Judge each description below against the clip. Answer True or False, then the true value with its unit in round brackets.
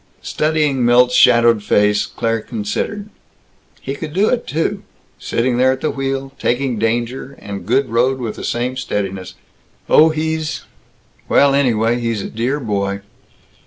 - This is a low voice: True (125 Hz)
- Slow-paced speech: False (145 wpm)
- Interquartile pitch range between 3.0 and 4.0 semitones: True (3.5 semitones)